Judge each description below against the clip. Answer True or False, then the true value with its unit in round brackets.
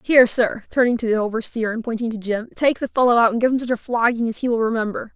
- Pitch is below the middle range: False (235 Hz)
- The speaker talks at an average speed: False (280 wpm)